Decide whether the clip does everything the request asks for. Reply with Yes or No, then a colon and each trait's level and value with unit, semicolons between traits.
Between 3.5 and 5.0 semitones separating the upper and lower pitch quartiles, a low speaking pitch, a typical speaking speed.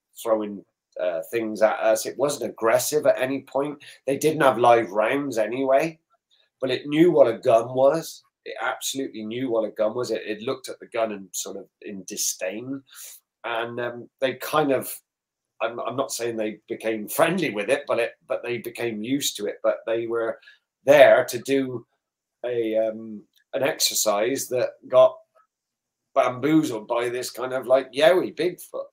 Yes: average, 4.0 semitones; low, 120 Hz; average, 170 wpm